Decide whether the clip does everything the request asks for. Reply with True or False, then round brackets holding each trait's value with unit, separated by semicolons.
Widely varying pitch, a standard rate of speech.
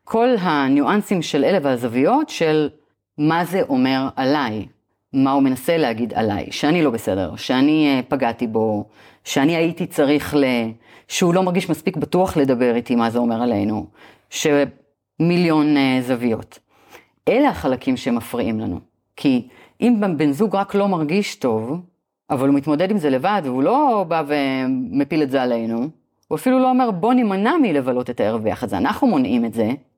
False (7.0 semitones; 155 wpm)